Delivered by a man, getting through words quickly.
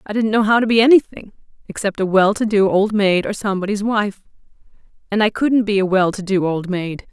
No: female; fast, 220 wpm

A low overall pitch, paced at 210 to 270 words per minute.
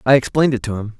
No: low, 125 Hz; fast, 300 wpm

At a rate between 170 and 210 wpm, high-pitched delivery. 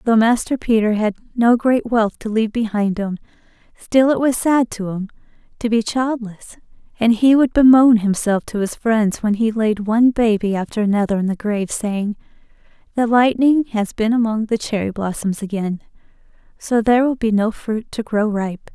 Yes: average, 180 wpm; high, 220 Hz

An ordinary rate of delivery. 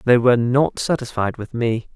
Yes: average, 185 wpm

